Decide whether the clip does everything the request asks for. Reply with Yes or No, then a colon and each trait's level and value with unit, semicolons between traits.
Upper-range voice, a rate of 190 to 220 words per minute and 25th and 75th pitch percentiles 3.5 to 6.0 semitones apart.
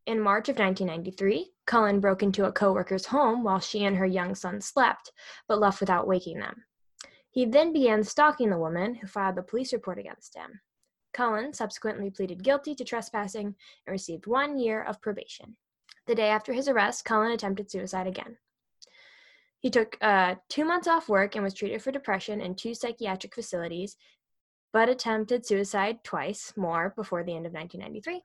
No: high, 210 Hz; average, 175 wpm; average, 3.9 semitones